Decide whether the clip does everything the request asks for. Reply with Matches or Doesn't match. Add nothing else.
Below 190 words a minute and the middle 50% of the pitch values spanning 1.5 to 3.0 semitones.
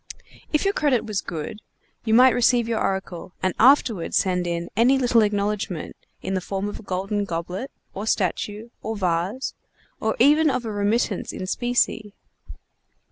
Doesn't match